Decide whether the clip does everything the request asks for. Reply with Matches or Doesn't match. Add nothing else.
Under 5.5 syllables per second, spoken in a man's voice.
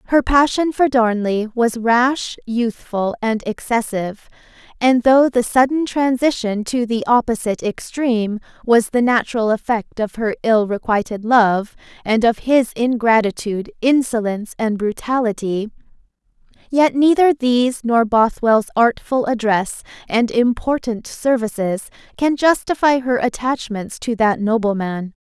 Doesn't match